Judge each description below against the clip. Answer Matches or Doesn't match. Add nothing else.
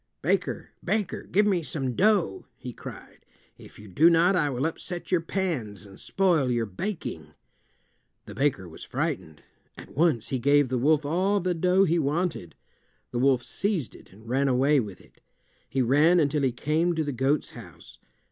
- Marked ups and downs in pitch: Matches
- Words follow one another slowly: Doesn't match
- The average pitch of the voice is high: Doesn't match